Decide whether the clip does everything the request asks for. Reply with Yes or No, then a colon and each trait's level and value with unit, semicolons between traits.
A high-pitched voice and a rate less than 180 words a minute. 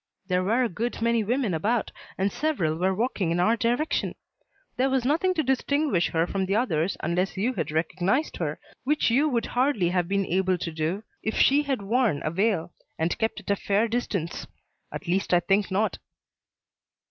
No: high, 205 Hz; average, 190 wpm